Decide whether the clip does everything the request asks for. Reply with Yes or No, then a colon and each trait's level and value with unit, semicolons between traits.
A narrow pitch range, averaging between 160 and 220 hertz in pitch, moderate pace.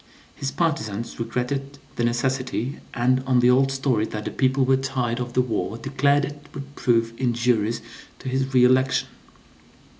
No: narrow, 2.2 semitones; low, 130 Hz; average, 160 wpm